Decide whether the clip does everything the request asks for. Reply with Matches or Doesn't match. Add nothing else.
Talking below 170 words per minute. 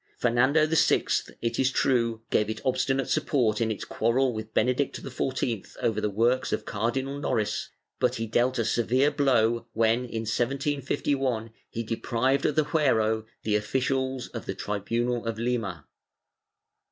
Matches